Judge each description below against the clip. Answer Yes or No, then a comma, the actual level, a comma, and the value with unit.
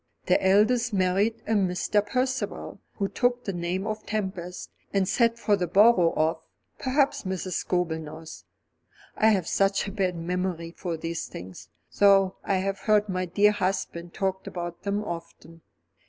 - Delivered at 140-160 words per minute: Yes, average, 155 wpm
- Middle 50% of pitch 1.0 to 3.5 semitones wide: Yes, average, 3.1 semitones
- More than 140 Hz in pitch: Yes, high, 190 Hz